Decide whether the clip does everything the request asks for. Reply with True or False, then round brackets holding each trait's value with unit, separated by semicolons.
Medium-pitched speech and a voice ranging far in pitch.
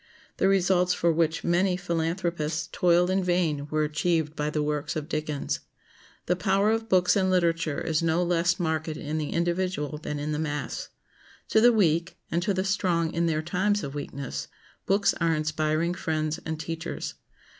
False (170 Hz; 2.7 semitones)